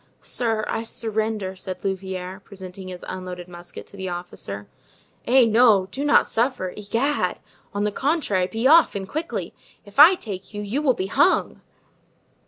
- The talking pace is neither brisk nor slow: Yes, average, 160 wpm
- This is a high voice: Yes, high, 205 Hz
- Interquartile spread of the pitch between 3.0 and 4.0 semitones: No, average, 4.6 semitones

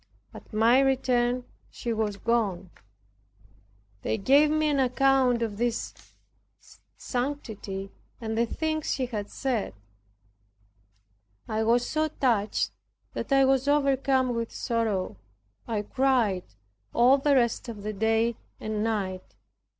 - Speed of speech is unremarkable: No, slow, 120 wpm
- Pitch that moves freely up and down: No, average, 3.7 semitones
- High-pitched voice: Yes, high, 235 Hz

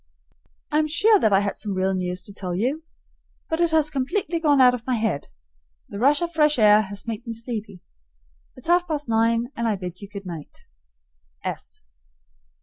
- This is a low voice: No, high, 230 Hz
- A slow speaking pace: No, average, 190 wpm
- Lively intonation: Yes, wide, 7.0 semitones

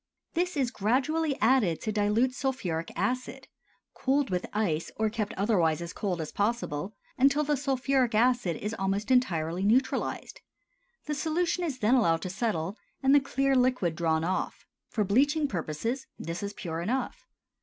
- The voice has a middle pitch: No, high, 225 Hz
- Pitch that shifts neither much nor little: No, wide, 6.4 semitones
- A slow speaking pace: No, average, 155 wpm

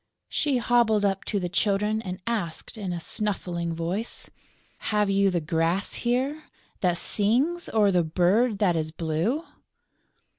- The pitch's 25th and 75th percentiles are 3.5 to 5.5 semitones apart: Yes, average, 4.5 semitones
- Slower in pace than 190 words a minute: Yes, average, 145 wpm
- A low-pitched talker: No, high, 200 Hz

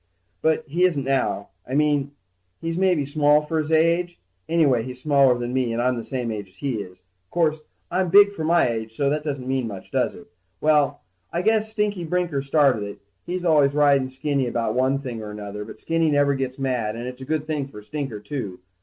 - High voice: No, medium, 140 Hz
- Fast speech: Yes, fast, 215 wpm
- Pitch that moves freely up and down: No, average, 4.2 semitones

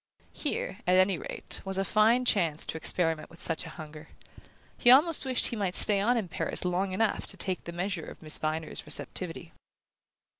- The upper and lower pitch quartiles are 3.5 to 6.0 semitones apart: Yes, average, 4.6 semitones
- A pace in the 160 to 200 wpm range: Yes, average, 190 wpm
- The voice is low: No, medium, 185 Hz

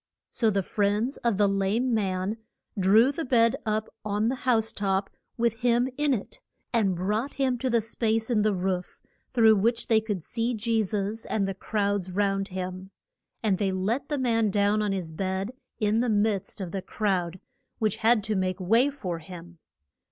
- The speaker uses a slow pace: No, average, 185 wpm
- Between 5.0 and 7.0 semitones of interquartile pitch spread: No, average, 3.0 semitones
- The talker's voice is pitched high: Yes, high, 210 Hz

